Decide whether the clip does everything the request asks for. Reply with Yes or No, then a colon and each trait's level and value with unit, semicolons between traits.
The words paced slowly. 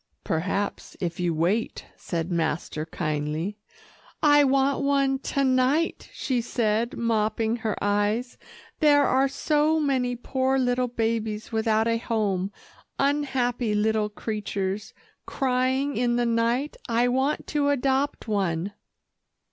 Yes: slow, 120 wpm